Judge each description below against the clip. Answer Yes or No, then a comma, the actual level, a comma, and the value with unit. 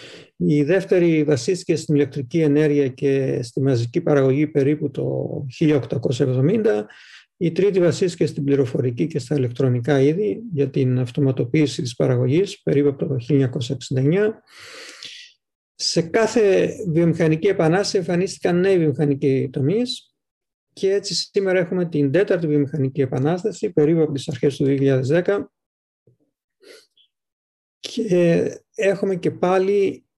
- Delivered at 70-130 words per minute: Yes, slow, 115 wpm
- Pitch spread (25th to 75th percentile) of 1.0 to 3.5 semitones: No, average, 5.2 semitones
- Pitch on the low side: No, medium, 155 Hz